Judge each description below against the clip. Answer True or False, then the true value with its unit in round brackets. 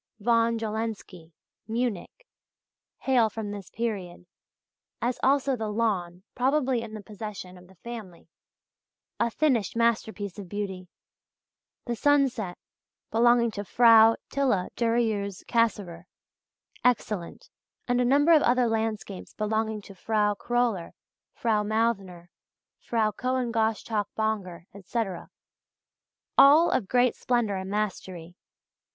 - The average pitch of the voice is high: True (220 Hz)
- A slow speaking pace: True (115 wpm)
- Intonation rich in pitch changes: False (3.1 semitones)